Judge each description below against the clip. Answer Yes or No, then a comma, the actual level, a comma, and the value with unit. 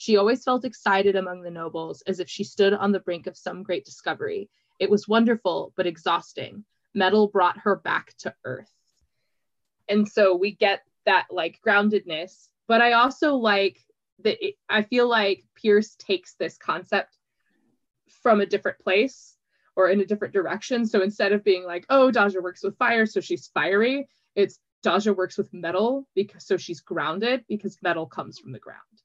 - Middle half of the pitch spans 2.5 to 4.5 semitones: Yes, average, 3.7 semitones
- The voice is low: No, high, 200 Hz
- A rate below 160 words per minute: No, average, 180 wpm